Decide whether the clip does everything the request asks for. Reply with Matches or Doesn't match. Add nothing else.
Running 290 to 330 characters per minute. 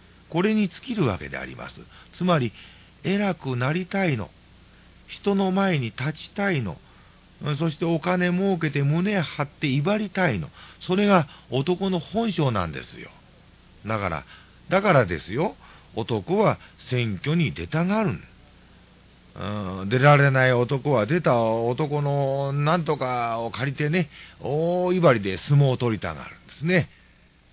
Doesn't match